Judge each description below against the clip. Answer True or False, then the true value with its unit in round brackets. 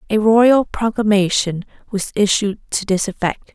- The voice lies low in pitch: False (205 Hz)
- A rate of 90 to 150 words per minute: True (135 wpm)